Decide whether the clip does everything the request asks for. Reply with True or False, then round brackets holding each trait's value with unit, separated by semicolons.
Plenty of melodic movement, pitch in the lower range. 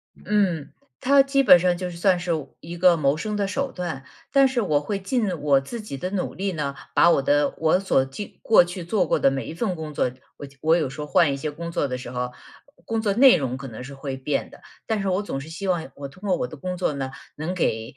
False (5.9 semitones; 170 Hz)